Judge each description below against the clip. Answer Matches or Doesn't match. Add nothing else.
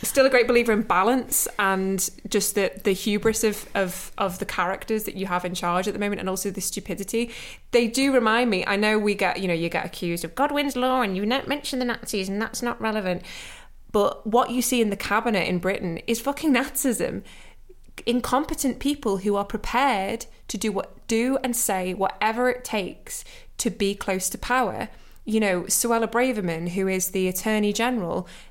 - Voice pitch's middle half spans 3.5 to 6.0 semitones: Matches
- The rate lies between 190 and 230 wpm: Matches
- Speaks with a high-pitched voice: Matches